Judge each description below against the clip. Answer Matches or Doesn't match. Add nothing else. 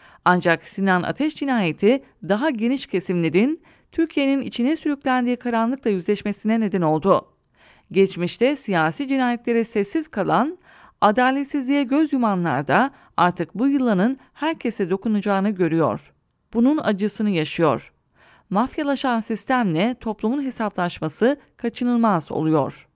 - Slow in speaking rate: Matches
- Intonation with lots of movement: Matches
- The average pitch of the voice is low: Doesn't match